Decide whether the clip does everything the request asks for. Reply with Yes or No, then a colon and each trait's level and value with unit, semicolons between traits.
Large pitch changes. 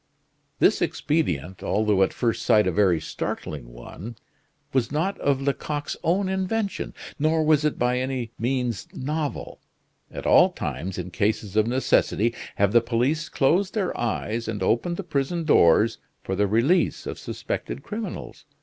Yes: wide, 6.7 semitones